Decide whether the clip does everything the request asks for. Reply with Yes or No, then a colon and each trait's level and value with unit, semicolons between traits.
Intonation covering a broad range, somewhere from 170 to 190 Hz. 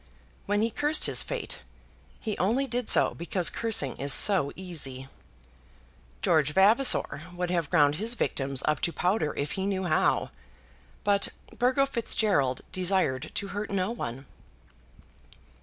Yes: wide, 6.7 semitones; medium, 185 Hz